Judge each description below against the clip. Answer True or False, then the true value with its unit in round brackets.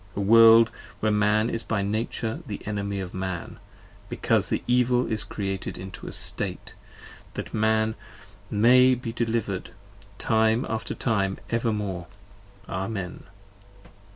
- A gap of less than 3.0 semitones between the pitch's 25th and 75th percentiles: True (2.5 semitones)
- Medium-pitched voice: False (110 Hz)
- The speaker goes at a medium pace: False (125 wpm)